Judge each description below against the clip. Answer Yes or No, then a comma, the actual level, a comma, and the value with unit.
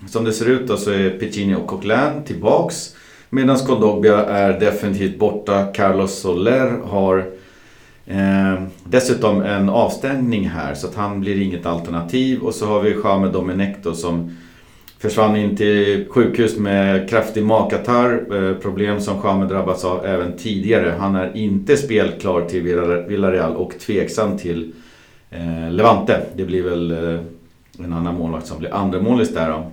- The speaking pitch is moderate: No, low, 100 Hz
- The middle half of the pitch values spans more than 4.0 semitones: No, average, 2.8 semitones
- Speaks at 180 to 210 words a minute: No, average, 150 wpm